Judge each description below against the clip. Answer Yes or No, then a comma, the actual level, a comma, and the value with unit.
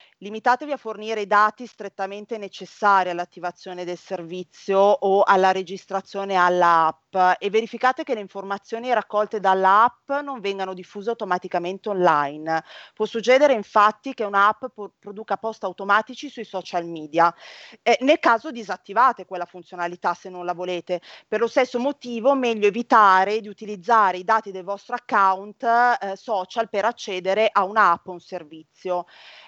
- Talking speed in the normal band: Yes, average, 140 wpm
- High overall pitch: Yes, high, 200 Hz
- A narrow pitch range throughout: No, average, 3.7 semitones